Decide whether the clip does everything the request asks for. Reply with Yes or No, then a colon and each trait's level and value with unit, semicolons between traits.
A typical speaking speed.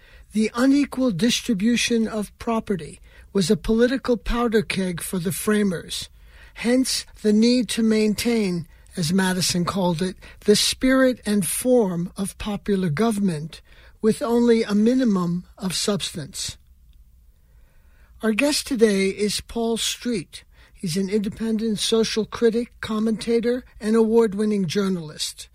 No: slow, 120 wpm